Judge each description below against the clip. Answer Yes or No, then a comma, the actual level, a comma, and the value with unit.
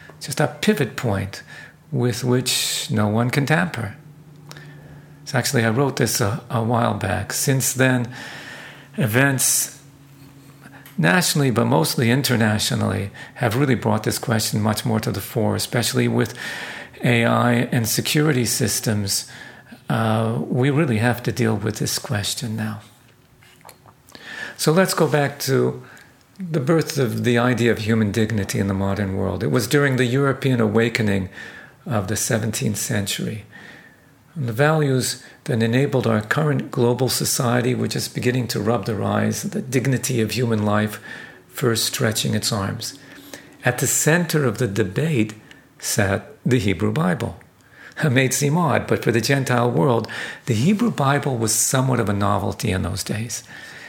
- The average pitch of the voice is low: Yes, low, 120 Hz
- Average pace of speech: Yes, average, 150 wpm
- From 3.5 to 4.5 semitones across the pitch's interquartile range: Yes, average, 4.0 semitones